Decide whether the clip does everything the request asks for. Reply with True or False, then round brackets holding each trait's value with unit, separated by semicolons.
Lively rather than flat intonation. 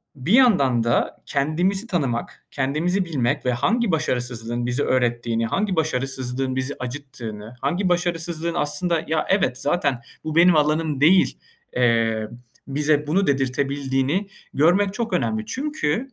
True (5.8 semitones)